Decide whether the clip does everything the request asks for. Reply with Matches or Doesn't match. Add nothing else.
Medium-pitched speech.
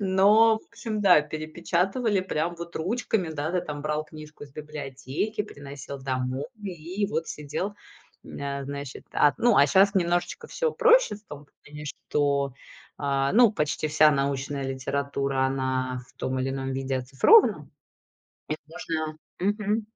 Matches